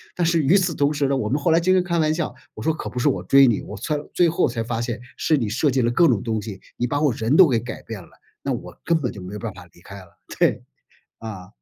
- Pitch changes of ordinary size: No, wide, 6.2 semitones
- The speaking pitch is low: Yes, low, 130 Hz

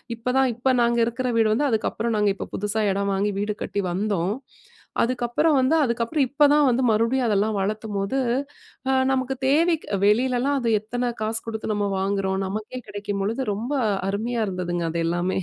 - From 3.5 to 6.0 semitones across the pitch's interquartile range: Yes, average, 3.9 semitones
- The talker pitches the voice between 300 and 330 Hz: No, high, 220 Hz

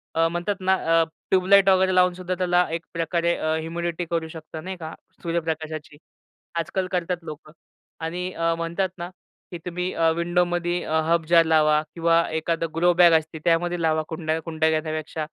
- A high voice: No, medium, 170 Hz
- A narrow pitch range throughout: Yes, narrow, 1.7 semitones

